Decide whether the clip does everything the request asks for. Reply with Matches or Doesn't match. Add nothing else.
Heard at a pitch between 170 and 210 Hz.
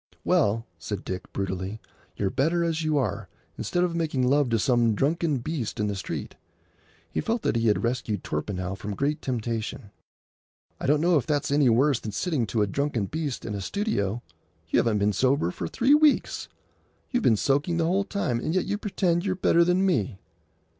Doesn't match